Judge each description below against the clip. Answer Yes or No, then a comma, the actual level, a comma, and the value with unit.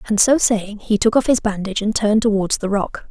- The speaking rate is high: Yes, fast, 250 wpm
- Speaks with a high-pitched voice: Yes, high, 210 Hz